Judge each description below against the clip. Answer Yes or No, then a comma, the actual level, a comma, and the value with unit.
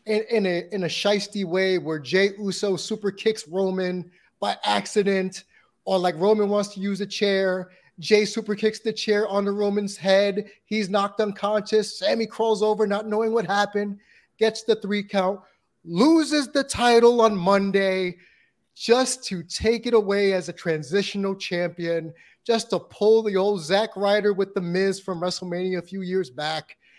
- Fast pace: No, average, 170 wpm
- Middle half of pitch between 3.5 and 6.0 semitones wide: No, narrow, 2.4 semitones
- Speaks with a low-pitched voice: No, high, 200 Hz